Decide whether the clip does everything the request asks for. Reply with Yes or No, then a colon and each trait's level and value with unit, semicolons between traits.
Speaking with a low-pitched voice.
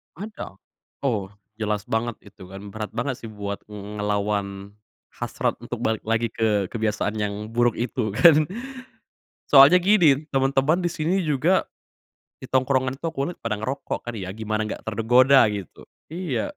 Yes: low, 115 Hz